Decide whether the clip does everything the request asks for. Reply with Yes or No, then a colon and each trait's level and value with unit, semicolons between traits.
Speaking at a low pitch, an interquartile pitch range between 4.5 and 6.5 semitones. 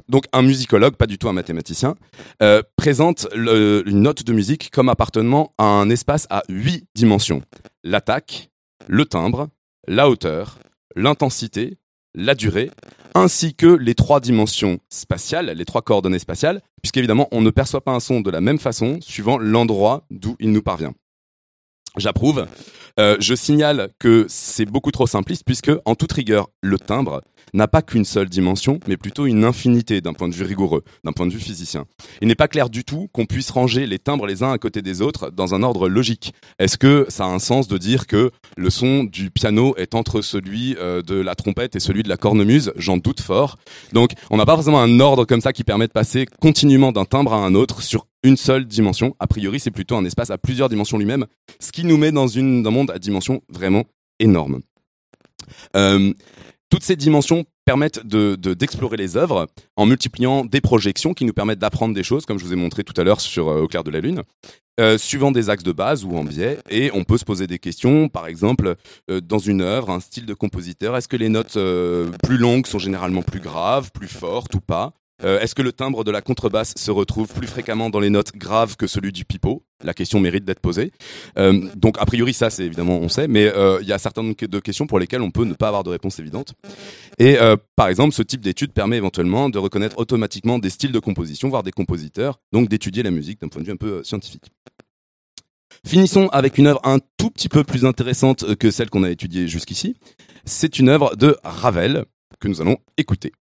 Yes: low, 110 Hz; average, 5.1 semitones